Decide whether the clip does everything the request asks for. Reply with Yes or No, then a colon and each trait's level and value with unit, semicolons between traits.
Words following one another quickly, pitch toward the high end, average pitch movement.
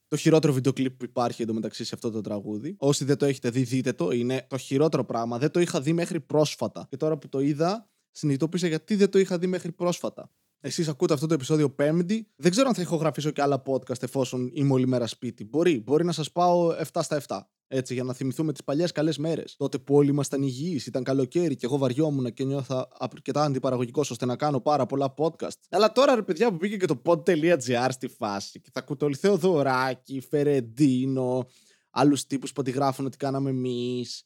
No: fast, 210 wpm; medium, 140 Hz; average, 3.8 semitones